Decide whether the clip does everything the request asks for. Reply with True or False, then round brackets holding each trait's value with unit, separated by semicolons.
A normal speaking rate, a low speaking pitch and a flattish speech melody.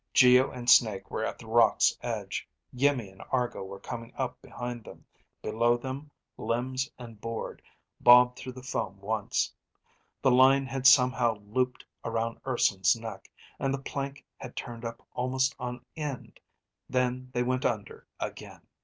True (155 wpm; 125 Hz; 2.1 semitones)